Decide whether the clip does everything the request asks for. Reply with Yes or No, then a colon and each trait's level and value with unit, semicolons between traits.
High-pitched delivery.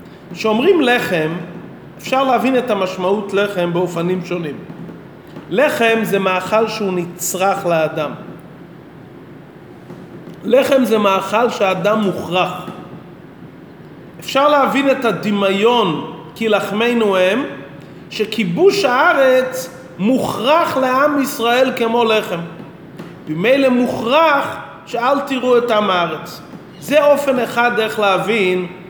Yes: high, 210 Hz